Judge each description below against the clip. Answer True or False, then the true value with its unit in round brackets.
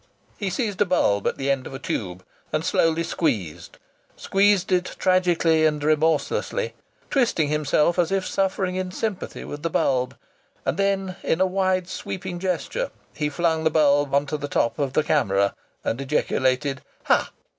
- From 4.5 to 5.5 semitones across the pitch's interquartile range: True (4.8 semitones)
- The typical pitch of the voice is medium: True (160 Hz)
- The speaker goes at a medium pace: True (165 wpm)